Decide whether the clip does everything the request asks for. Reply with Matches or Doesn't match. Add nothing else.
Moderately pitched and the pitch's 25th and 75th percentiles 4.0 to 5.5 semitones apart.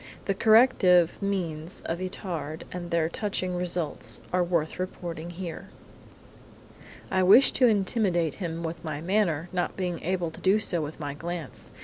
Doesn't match